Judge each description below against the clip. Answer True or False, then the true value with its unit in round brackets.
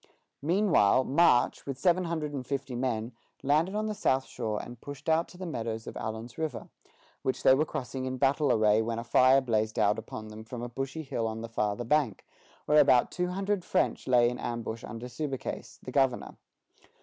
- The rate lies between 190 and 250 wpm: True (195 wpm)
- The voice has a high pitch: False (130 Hz)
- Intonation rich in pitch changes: False (4.7 semitones)